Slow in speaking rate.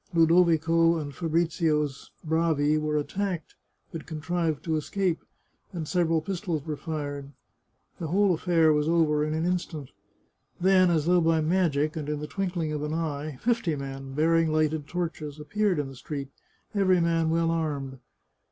No: average, 155 wpm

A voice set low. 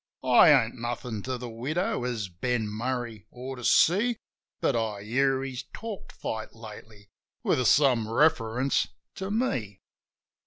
Yes: low, 125 Hz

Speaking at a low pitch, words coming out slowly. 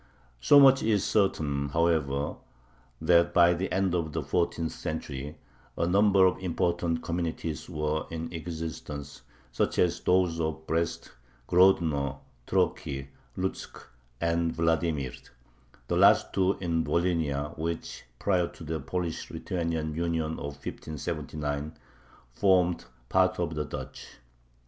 Yes: very low, 85 Hz; slow, 120 wpm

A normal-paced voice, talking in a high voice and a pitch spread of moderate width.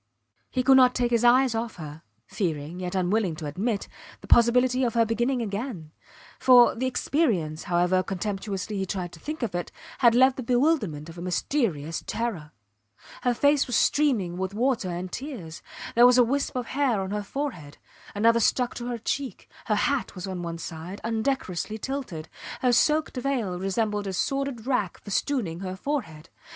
No: average, 175 wpm; high, 225 Hz; wide, 5.8 semitones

